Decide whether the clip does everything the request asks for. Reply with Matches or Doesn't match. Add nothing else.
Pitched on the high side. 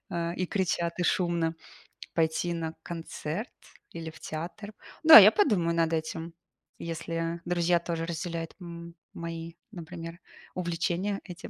Doesn't match